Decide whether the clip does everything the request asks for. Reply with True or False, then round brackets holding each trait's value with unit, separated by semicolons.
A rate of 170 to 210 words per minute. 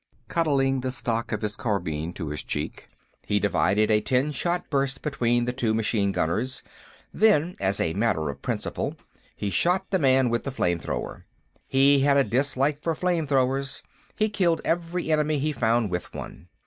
True (175 wpm)